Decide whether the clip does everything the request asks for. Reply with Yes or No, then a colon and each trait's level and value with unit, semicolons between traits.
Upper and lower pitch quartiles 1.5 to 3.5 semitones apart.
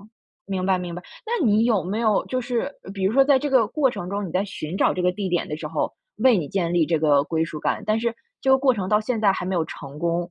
No: average, 5.2 semitones